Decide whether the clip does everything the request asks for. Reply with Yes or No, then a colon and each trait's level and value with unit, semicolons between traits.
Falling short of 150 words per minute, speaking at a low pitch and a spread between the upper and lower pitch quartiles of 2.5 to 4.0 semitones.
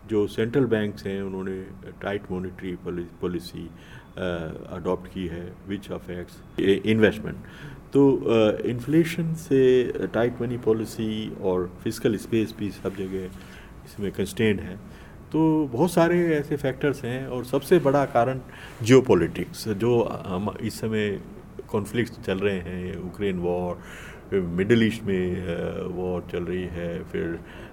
No: average, 130 wpm; low, 105 Hz; average, 4.8 semitones